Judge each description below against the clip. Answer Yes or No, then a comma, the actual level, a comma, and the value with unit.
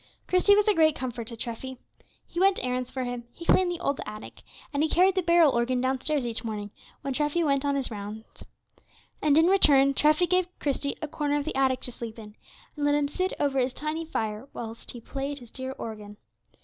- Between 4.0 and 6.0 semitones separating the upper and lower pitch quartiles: Yes, average, 4.6 semitones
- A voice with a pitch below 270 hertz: No, very high, 275 Hz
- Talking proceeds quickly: Yes, fast, 220 wpm